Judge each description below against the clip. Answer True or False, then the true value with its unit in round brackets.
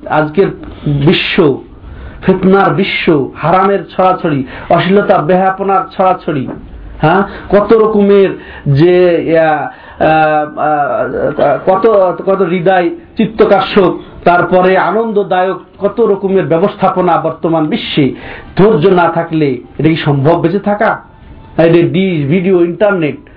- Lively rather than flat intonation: False (3.1 semitones)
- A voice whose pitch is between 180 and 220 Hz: True (185 Hz)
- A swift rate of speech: False (90 wpm)